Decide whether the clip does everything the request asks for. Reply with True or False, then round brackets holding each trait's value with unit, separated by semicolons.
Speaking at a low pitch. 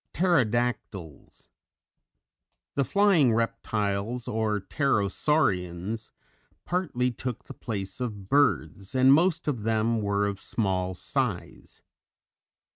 True (115 Hz)